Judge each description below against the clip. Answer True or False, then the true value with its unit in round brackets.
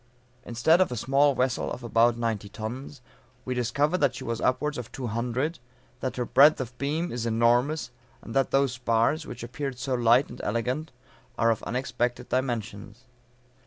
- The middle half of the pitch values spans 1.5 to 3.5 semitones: True (2.8 semitones)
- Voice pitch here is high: False (125 Hz)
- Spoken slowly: False (170 wpm)